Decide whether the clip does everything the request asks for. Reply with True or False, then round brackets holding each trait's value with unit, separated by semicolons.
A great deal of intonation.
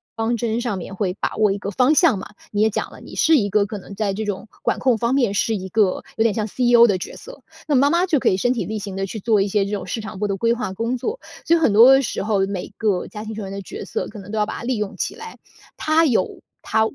False (3.6 semitones)